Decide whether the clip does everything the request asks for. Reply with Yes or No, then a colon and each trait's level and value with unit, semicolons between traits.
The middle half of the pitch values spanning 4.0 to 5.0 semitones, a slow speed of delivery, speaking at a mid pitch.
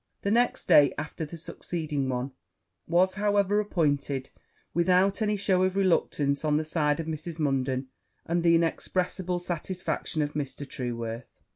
No: average, 4.4 semitones; average, 145 wpm; medium, 165 Hz